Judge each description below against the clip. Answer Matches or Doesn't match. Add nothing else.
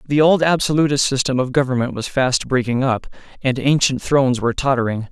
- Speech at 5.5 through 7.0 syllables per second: Matches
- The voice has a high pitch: Doesn't match